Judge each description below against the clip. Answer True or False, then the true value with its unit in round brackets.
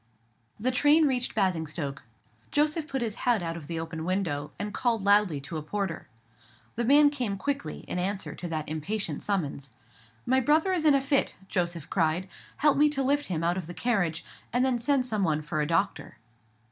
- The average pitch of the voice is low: False (200 Hz)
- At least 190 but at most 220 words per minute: True (195 wpm)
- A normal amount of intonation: False (8.1 semitones)